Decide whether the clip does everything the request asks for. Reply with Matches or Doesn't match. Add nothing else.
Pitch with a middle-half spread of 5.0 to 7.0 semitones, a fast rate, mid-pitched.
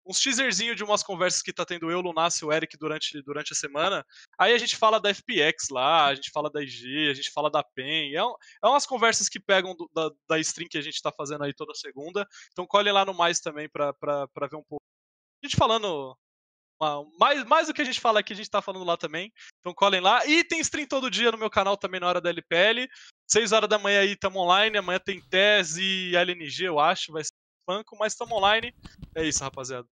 Matches